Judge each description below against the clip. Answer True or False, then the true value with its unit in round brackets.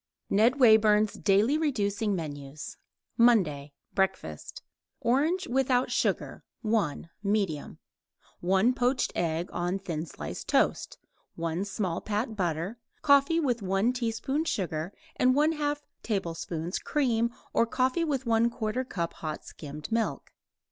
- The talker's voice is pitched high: True (215 Hz)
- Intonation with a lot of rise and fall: True (6.5 semitones)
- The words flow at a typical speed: False (115 wpm)